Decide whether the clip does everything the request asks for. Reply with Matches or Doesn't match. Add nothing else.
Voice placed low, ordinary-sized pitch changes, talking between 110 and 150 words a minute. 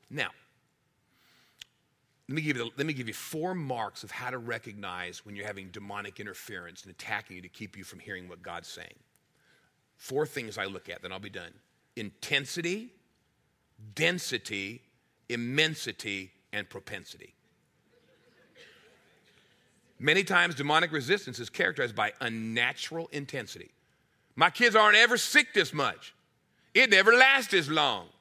Doesn't match